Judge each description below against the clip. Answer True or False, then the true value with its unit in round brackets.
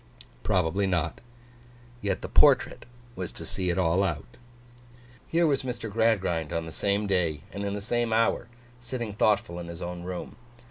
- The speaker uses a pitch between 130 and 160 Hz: False (95 Hz)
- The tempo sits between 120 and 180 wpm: True (170 wpm)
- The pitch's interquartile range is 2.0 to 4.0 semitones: False (4.4 semitones)